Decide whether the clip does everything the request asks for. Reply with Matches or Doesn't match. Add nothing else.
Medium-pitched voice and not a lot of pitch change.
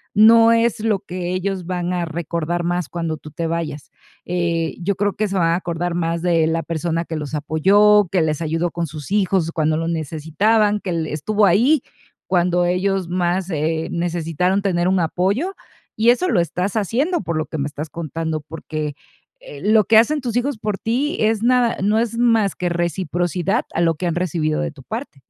Doesn't match